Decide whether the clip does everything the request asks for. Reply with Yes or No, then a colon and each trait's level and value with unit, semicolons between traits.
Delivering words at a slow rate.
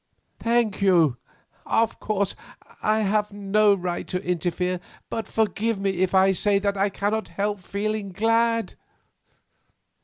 Yes: slow, 130 wpm